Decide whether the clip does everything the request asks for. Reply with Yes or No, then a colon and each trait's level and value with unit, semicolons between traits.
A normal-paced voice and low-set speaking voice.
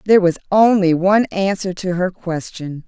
No: average, 165 wpm; medium, 185 Hz